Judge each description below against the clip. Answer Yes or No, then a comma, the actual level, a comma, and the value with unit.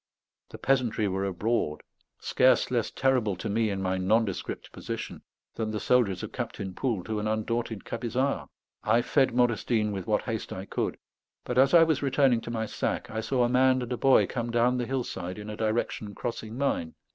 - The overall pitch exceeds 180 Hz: No, low, 115 Hz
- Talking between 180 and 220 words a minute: Yes, average, 195 wpm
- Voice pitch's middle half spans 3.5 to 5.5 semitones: No, average, 3.1 semitones